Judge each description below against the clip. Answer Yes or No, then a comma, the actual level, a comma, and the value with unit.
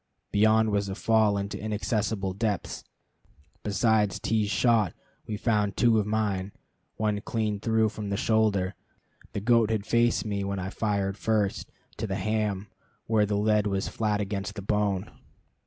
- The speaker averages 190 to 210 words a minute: No, average, 160 wpm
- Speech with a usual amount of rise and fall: No, narrow, 1.7 semitones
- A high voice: No, low, 105 Hz